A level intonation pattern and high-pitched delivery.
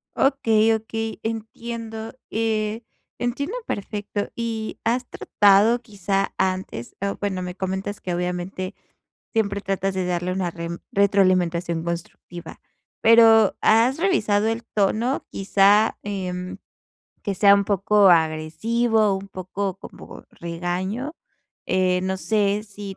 No: average, 3.2 semitones; high, 200 Hz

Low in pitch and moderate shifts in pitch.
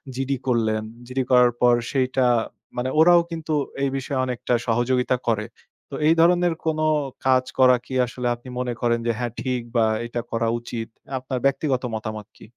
No: low, 125 Hz; narrow, 2.1 semitones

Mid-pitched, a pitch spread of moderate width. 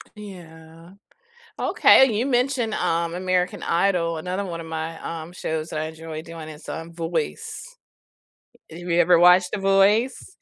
Yes: medium, 175 Hz; average, 3.2 semitones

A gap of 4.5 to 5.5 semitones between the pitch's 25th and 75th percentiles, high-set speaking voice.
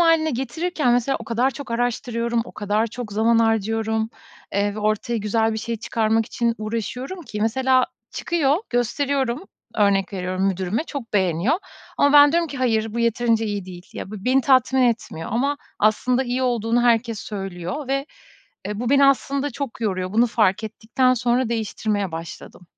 No: average, 3.4 semitones; high, 230 Hz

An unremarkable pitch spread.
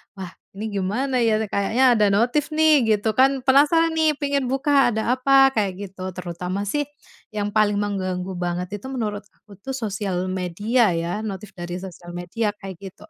No: wide, 5.8 semitones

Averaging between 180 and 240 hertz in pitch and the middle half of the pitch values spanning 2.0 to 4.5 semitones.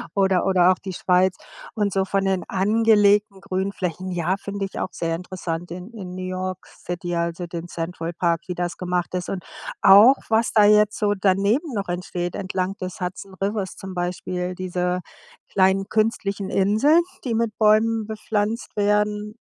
Yes: high, 190 Hz; narrow, 2.5 semitones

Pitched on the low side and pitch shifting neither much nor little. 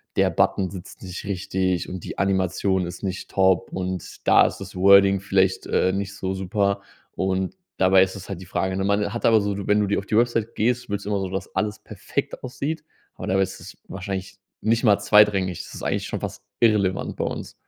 No: very low, 95 Hz; narrow, 1.7 semitones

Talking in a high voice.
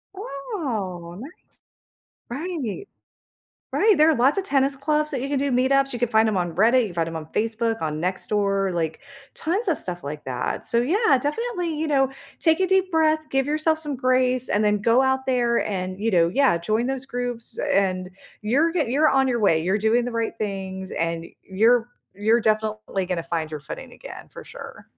Yes: high, 240 Hz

